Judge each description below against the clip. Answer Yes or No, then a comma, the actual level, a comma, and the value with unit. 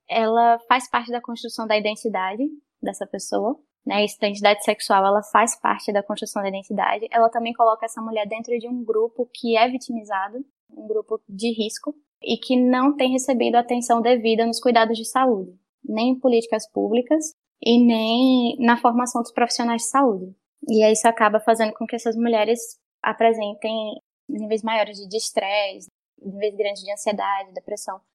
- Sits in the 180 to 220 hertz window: No, high, 230 Hz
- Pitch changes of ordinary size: No, narrow, 2.2 semitones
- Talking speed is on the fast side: No, average, 165 wpm